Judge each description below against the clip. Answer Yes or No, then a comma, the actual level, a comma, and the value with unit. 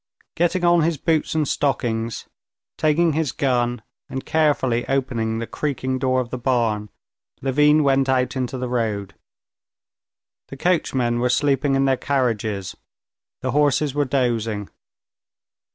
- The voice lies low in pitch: Yes, low, 130 Hz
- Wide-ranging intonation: No, average, 3.5 semitones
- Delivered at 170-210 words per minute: No, slow, 135 wpm